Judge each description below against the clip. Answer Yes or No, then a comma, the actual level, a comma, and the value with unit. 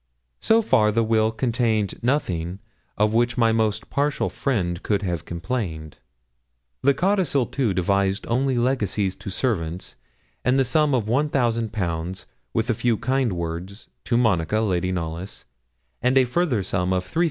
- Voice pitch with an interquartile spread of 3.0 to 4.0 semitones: No, wide, 5.4 semitones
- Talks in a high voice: No, low, 110 Hz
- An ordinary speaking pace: Yes, average, 150 wpm